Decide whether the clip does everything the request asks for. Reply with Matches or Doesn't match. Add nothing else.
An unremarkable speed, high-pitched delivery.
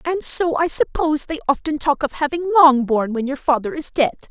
Doesn't match